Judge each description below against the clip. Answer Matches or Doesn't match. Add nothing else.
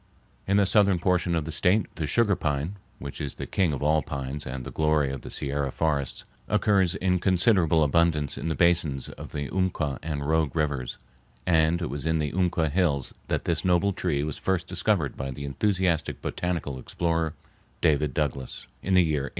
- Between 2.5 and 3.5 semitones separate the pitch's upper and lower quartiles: Doesn't match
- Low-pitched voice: Matches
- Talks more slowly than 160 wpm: Doesn't match